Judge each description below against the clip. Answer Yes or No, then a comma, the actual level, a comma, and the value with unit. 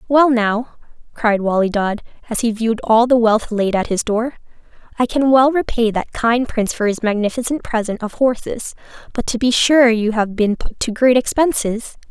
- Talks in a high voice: Yes, high, 230 Hz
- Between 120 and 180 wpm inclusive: No, average, 195 wpm